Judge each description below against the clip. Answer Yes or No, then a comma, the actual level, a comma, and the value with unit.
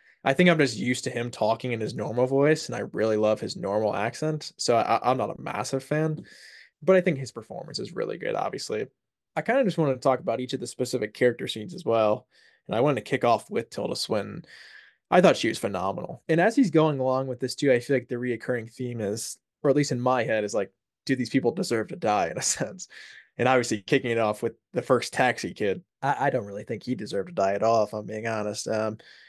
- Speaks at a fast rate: Yes, fast, 250 wpm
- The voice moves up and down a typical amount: Yes, average, 3.3 semitones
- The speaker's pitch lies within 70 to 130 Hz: Yes, low, 125 Hz